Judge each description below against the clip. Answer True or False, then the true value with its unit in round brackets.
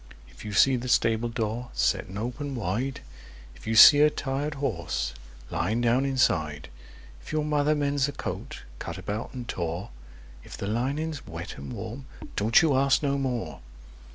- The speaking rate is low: False (155 wpm)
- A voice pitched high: False (125 Hz)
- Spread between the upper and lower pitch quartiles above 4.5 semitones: True (4.9 semitones)